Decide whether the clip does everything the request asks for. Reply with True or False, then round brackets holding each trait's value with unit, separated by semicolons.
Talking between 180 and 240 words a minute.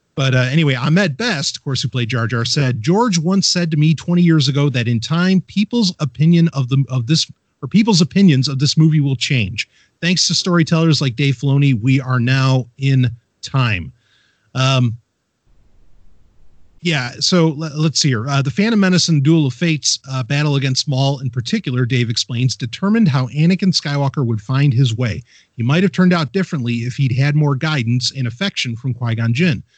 True (190 wpm)